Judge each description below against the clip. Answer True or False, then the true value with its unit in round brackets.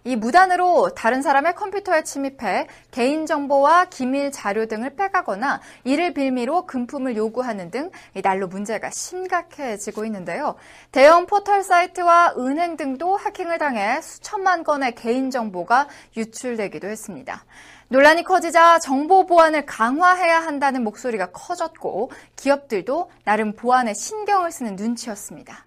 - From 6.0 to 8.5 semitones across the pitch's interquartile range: True (6.7 semitones)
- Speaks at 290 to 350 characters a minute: True (325 characters per minute)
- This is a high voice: True (280 Hz)